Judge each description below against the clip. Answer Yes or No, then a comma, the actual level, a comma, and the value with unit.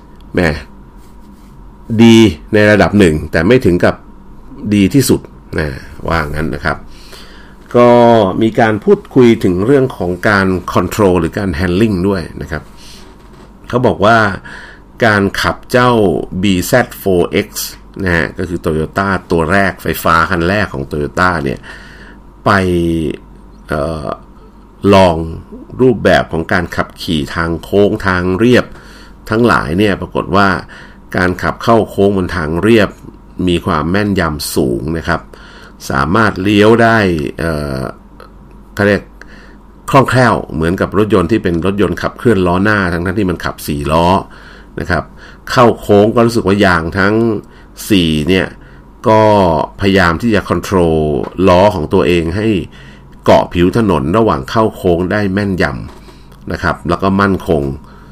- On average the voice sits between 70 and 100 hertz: Yes, very low, 95 Hz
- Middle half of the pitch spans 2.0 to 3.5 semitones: No, average, 4.3 semitones